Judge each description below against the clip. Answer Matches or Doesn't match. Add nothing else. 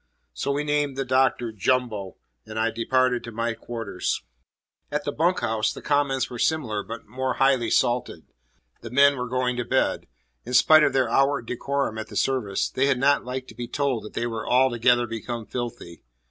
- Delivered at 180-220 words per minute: Matches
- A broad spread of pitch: Doesn't match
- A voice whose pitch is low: Matches